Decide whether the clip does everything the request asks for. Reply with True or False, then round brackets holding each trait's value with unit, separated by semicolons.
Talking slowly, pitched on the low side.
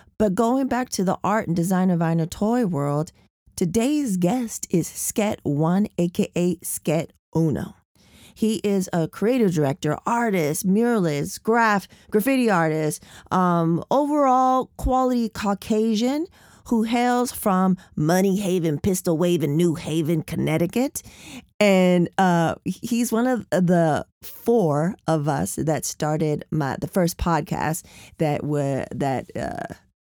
False (130 wpm; 185 Hz)